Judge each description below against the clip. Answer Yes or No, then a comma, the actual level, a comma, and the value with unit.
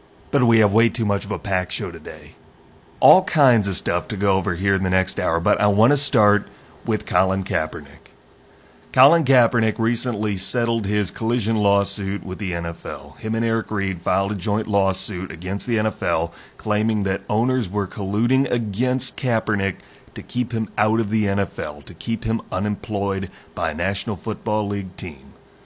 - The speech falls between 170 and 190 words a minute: Yes, average, 180 wpm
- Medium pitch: No, low, 105 Hz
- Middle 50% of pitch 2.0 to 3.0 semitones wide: Yes, narrow, 2.6 semitones